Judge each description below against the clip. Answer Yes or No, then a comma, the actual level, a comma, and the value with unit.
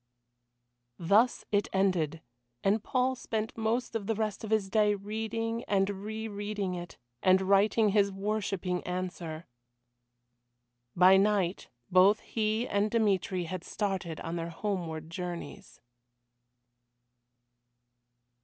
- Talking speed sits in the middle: No, slow, 115 wpm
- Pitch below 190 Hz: No, high, 200 Hz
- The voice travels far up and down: No, average, 2.9 semitones